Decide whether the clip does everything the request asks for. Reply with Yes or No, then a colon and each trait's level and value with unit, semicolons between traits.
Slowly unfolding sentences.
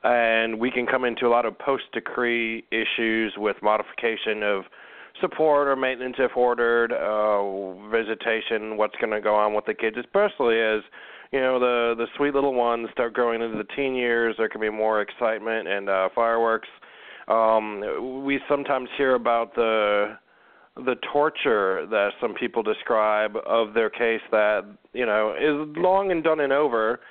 No: average, 165 wpm